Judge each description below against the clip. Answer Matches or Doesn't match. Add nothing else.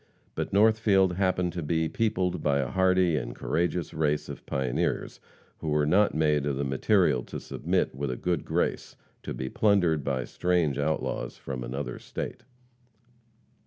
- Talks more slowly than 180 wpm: Matches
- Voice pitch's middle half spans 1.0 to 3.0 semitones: Doesn't match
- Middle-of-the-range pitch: Doesn't match